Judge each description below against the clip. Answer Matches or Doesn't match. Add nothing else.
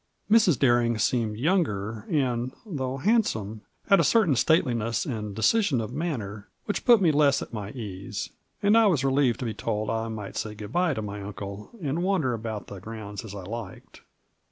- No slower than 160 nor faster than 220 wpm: Matches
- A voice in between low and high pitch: Doesn't match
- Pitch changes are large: Matches